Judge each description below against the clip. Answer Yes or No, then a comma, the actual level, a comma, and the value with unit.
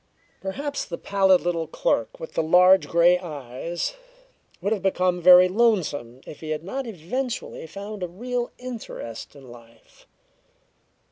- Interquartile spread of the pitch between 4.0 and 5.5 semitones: Yes, average, 4.5 semitones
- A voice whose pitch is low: No, medium, 180 Hz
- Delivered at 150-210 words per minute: No, average, 140 wpm